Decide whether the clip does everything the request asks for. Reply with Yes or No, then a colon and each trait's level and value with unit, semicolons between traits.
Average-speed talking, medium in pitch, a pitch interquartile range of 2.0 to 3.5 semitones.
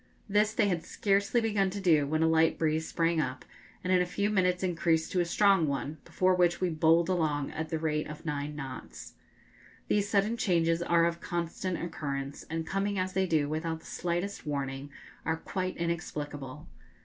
Yes: average, 185 wpm; medium, 170 Hz; average, 3.1 semitones